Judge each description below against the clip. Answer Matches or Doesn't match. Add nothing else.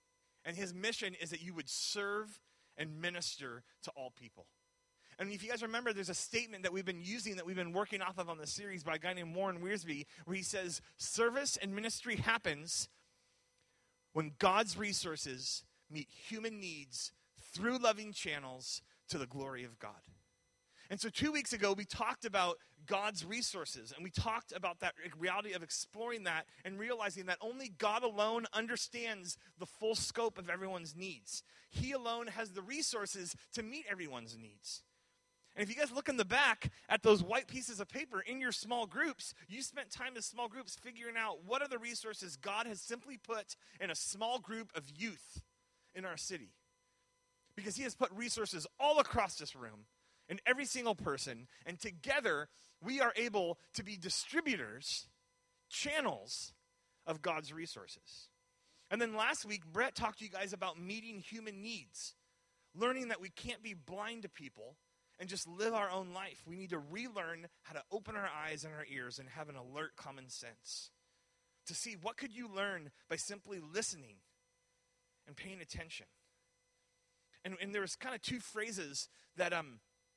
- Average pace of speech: Matches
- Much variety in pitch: Matches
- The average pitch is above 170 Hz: Matches